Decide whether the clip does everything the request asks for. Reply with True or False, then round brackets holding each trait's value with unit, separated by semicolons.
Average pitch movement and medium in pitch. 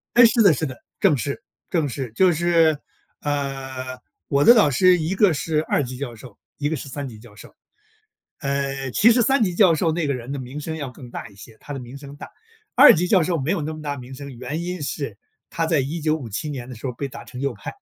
True (4.1 semitones; 145 Hz)